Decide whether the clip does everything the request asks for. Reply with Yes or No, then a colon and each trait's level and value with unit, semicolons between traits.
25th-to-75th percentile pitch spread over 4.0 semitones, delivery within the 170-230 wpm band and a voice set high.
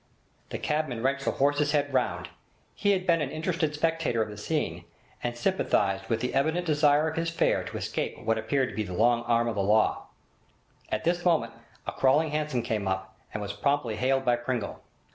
No: average, 5.3 semitones; average, 200 wpm; low, 135 Hz